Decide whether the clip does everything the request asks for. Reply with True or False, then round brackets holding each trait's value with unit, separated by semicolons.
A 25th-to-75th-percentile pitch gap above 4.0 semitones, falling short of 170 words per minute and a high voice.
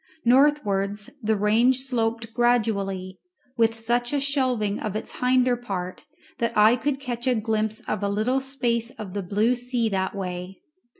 False (3.4 semitones; 160 wpm; 225 Hz)